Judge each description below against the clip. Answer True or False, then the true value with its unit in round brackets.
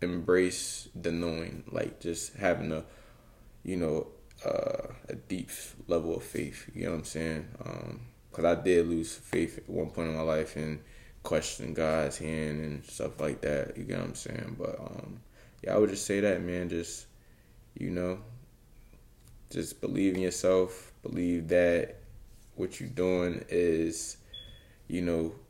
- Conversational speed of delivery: True (165 wpm)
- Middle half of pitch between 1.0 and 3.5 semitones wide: False (3.9 semitones)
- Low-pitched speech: True (85 Hz)